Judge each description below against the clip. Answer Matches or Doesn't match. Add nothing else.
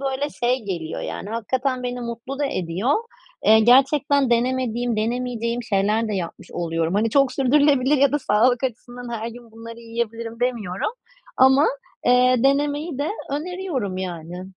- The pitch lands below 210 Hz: Doesn't match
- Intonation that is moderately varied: Matches